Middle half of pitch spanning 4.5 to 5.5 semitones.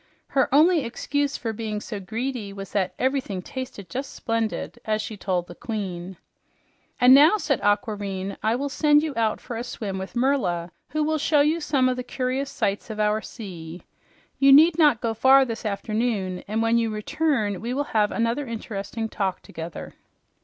Yes: average, 5.0 semitones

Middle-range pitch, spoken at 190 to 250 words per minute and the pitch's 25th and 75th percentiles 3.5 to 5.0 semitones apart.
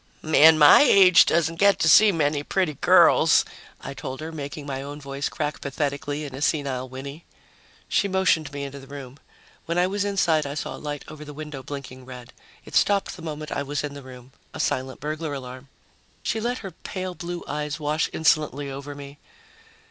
No: medium, 150 Hz; average, 200 wpm; average, 2.7 semitones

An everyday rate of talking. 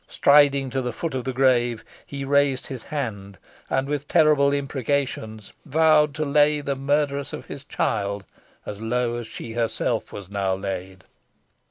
Yes: average, 160 wpm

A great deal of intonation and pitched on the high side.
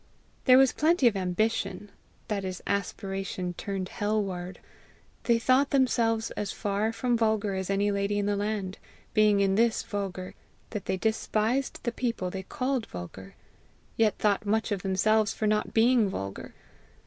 No: average, 2.8 semitones; high, 210 Hz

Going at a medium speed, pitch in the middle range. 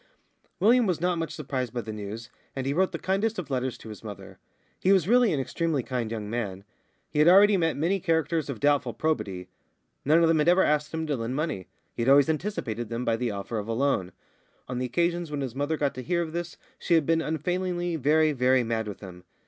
No: fast, 235 wpm; medium, 145 Hz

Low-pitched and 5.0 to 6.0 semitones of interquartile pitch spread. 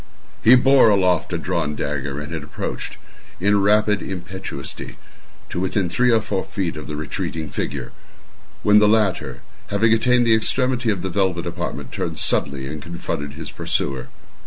Yes: very low, 95 Hz; wide, 5.4 semitones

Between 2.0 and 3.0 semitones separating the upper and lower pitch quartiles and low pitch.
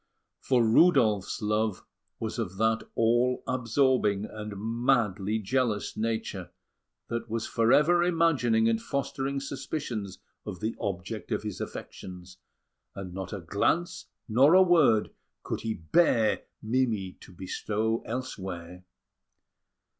No: average, 4.1 semitones; low, 110 Hz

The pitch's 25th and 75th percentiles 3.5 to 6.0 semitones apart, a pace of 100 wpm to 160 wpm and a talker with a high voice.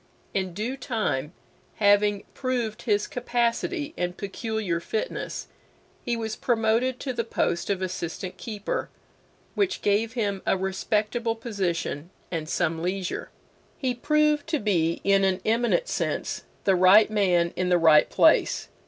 Yes: average, 4.3 semitones; slow, 135 wpm; high, 210 Hz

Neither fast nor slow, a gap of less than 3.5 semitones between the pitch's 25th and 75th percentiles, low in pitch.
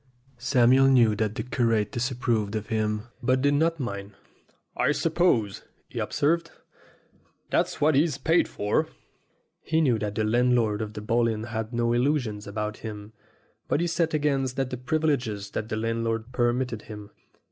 No: average, 160 wpm; average, 3.8 semitones; low, 120 Hz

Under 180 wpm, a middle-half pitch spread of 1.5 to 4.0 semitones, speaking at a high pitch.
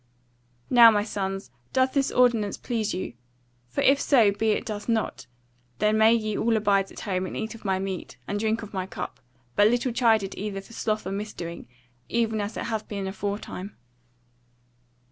No: average, 185 wpm; narrow, 2.6 semitones; high, 215 Hz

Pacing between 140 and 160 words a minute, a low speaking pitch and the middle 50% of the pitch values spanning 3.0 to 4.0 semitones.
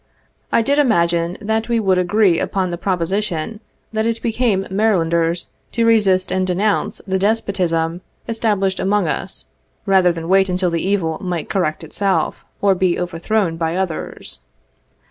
No: average, 150 wpm; high, 190 Hz; average, 3.6 semitones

